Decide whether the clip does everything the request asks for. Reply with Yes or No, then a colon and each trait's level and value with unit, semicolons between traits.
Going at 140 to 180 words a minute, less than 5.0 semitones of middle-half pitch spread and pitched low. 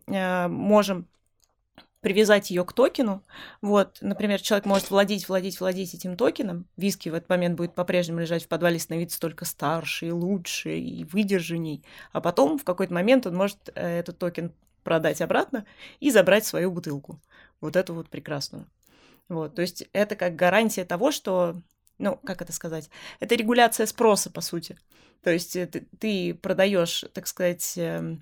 No: average, 155 wpm; average, 2.8 semitones; medium, 180 Hz